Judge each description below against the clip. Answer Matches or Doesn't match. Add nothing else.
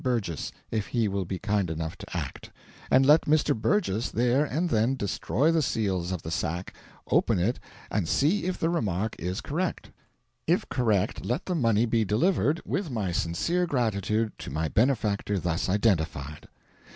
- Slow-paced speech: Doesn't match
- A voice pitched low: Matches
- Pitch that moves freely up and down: Matches